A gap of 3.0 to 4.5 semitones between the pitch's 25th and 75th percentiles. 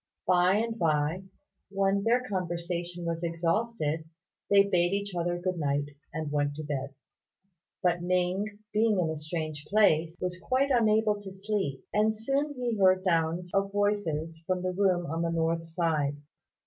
Yes: average, 3.8 semitones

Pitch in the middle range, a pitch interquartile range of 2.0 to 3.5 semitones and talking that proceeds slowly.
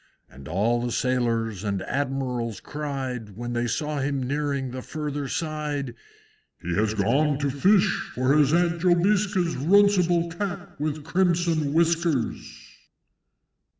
No: medium, 145 Hz; wide, 5.6 semitones; slow, 125 wpm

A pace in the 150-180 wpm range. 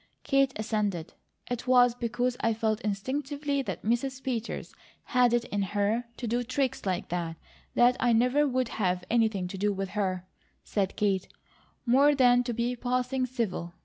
Yes: average, 165 wpm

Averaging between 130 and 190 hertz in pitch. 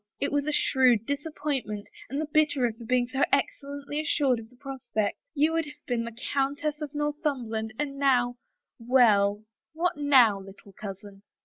No: very high, 265 Hz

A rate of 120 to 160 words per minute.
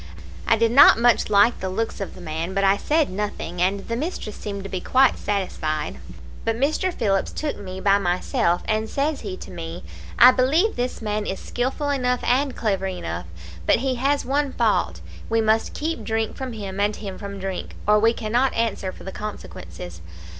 No: average, 190 wpm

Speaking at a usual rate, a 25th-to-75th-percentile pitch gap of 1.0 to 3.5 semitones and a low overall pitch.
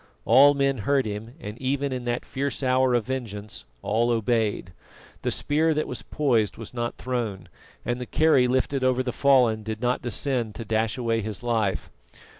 Yes: average, 180 wpm; average, 3.1 semitones; low, 120 Hz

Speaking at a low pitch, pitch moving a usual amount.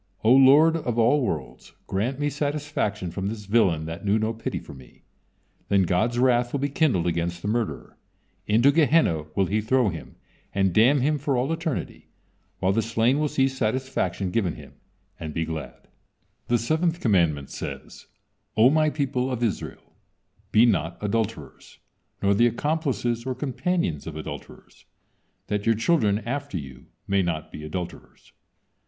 No: low, 115 Hz; wide, 6.4 semitones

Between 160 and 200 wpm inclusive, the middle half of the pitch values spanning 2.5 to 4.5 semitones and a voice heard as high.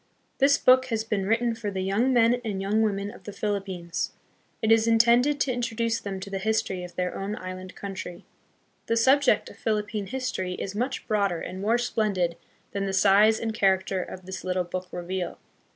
Yes: average, 195 wpm; average, 3.4 semitones; high, 205 Hz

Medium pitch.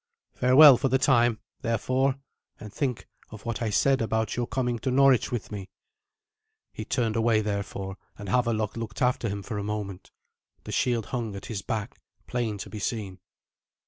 No: low, 115 Hz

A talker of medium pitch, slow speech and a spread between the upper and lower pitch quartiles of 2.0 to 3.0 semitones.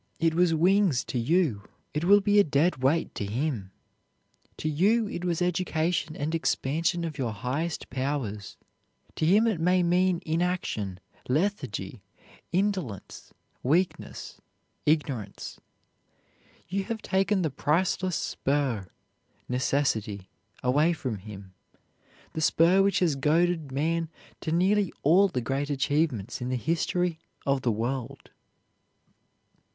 No: medium, 155 Hz; slow, 125 wpm; wide, 5.6 semitones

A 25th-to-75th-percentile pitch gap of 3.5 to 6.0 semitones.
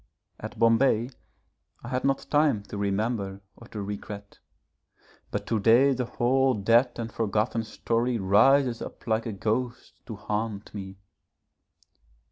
No: average, 3.1 semitones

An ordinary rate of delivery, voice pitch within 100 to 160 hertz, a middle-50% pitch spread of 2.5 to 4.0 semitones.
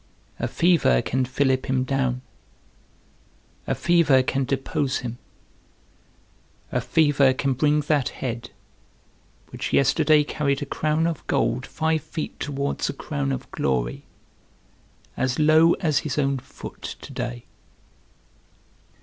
No: slow, 125 wpm; medium, 140 Hz; average, 3.0 semitones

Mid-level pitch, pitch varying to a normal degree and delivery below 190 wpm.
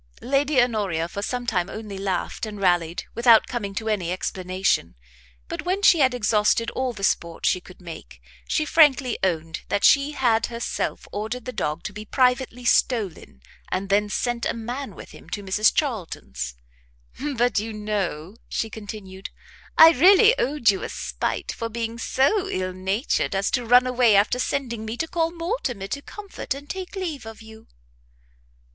No: high, 225 Hz; average, 4.8 semitones; average, 170 wpm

